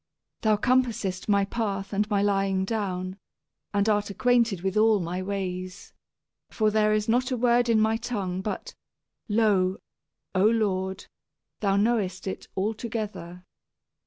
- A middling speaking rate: Yes, average, 145 wpm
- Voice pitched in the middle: No, high, 205 Hz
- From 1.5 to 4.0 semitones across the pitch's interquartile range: Yes, average, 2.7 semitones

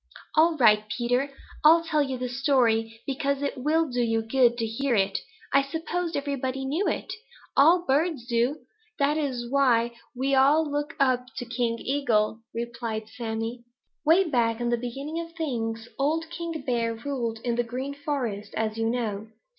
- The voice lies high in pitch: Yes, very high, 255 Hz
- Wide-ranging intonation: No, average, 3.7 semitones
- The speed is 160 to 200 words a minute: Yes, average, 170 wpm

